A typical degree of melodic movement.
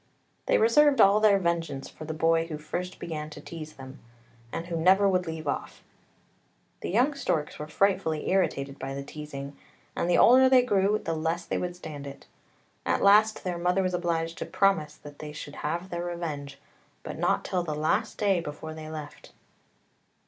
Yes: average, 3.9 semitones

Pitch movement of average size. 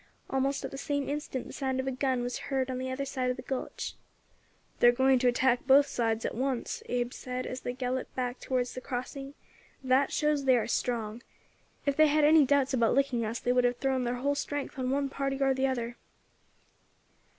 No: narrow, 1.8 semitones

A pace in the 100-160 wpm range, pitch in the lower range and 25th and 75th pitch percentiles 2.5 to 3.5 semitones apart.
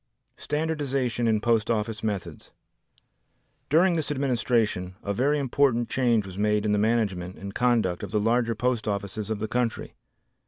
Yes: average, 155 wpm; low, 115 Hz; average, 3.2 semitones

